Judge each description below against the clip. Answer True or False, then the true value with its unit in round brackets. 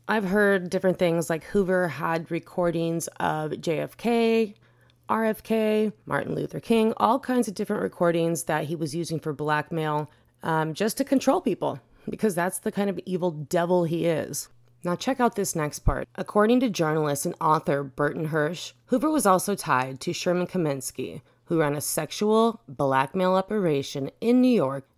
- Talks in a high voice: False (175 Hz)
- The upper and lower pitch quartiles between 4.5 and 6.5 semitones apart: True (5.5 semitones)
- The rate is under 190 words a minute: True (165 wpm)